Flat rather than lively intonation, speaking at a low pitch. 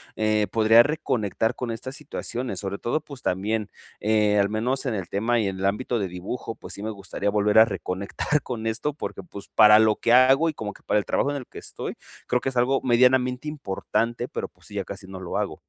No: average, 3.8 semitones; low, 110 Hz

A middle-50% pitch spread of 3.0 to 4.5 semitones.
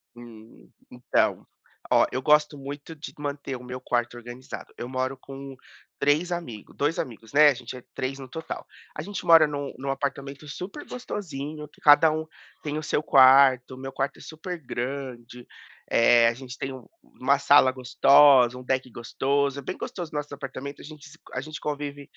No: narrow, 2.5 semitones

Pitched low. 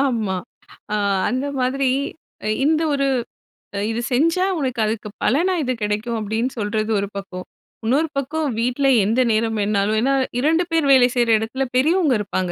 No: high, 245 Hz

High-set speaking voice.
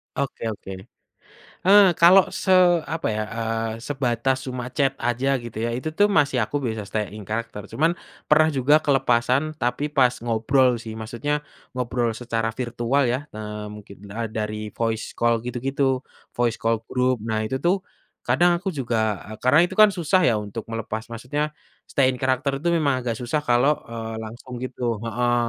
No: low, 125 Hz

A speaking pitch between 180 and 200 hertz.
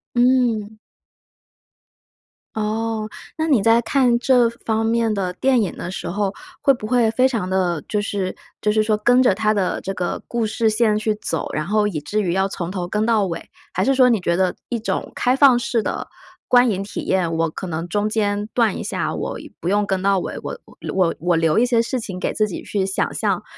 No: high, 215 Hz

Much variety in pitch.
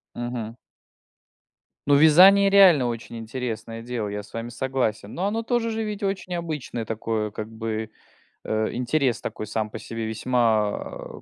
Yes: wide, 6.3 semitones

